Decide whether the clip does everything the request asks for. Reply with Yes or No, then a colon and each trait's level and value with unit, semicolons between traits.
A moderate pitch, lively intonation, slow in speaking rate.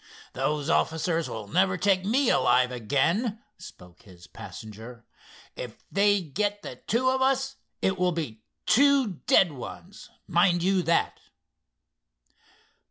Yes: medium, 180 Hz; wide, 7.4 semitones; slow, 125 wpm